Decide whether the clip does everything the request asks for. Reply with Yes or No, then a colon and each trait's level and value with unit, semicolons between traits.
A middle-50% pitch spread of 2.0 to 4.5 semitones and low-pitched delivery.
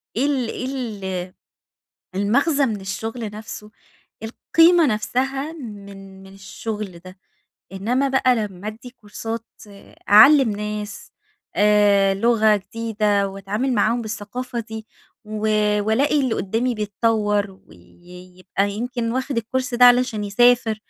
No: average, 3.5 semitones; high, 220 Hz